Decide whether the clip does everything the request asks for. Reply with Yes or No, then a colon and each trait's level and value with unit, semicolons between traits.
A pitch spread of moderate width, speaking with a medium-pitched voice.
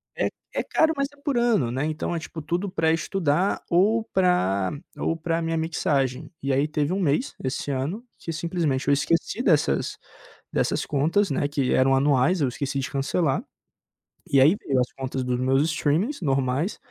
Yes: average, 4.7 semitones; medium, 150 Hz